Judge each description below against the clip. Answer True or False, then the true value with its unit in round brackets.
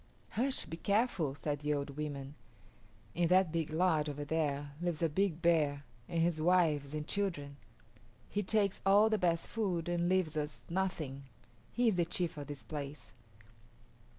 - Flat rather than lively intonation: False (3.9 semitones)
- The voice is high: False (165 Hz)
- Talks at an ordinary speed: True (165 wpm)